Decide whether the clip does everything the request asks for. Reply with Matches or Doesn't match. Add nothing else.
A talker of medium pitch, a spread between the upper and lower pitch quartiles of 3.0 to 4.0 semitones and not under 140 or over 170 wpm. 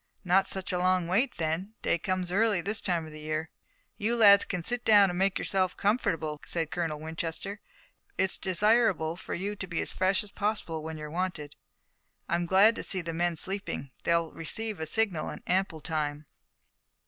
Doesn't match